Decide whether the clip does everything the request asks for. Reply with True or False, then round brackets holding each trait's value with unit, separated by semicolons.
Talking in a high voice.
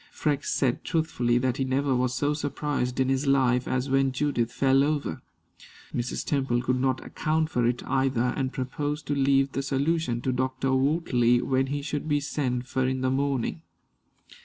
False (135 Hz)